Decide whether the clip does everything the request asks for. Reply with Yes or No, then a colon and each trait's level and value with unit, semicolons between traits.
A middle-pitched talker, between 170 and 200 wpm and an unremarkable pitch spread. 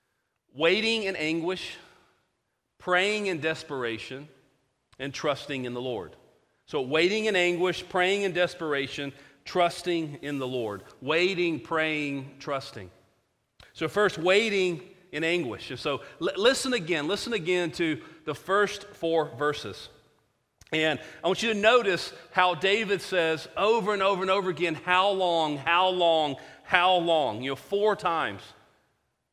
No: medium, 165 Hz; slow, 135 wpm; average, 4.0 semitones